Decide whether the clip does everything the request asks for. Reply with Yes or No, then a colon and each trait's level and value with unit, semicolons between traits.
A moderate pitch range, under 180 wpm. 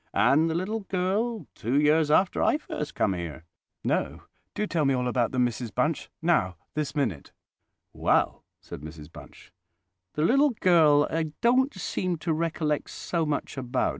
No: wide, 6.0 semitones; average, 160 wpm